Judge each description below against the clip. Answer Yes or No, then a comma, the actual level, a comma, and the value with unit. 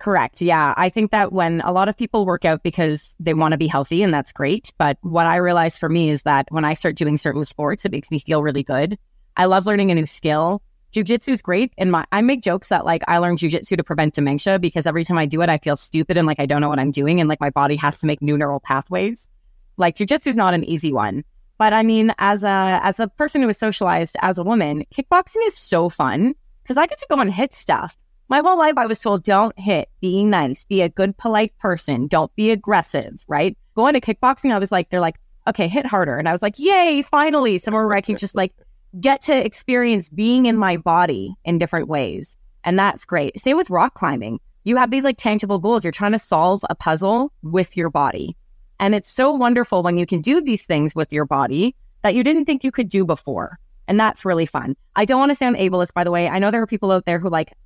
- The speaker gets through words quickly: Yes, fast, 250 wpm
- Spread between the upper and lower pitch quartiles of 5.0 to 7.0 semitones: Yes, average, 5.3 semitones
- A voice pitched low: No, medium, 185 Hz